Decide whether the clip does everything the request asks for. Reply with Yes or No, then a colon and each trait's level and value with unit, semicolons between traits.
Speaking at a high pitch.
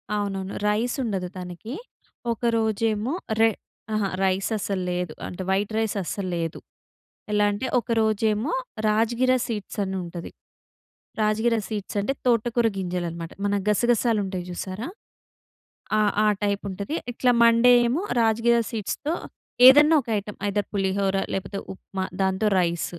Yes: high, 210 Hz